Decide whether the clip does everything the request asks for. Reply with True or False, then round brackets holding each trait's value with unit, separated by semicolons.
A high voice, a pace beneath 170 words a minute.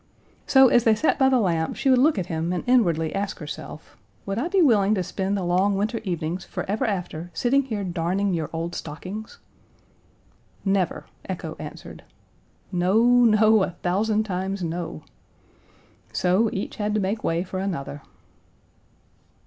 True (195 Hz; 155 wpm)